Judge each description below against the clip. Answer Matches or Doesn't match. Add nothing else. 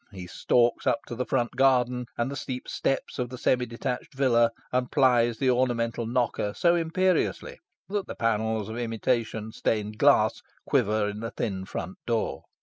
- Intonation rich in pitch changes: Doesn't match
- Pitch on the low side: Matches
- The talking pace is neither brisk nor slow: Matches